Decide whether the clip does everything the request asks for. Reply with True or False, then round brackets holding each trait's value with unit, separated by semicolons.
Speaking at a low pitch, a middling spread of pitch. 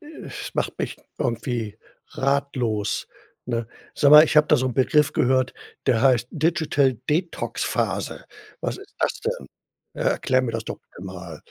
True (130 Hz; 4.5 semitones)